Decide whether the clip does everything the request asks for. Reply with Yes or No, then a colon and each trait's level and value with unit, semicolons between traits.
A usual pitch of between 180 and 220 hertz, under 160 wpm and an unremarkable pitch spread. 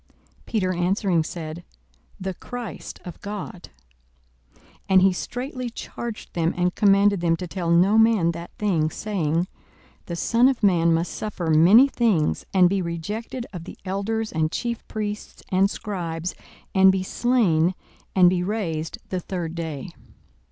Yes: medium, 185 Hz; average, 150 wpm; average, 3.8 semitones